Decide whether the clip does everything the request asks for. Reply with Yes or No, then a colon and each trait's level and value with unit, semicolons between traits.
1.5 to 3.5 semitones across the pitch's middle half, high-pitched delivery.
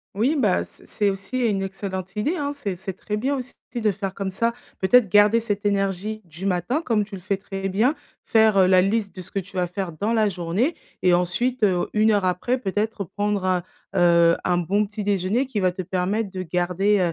Yes: average, 2.9 semitones; high, 195 Hz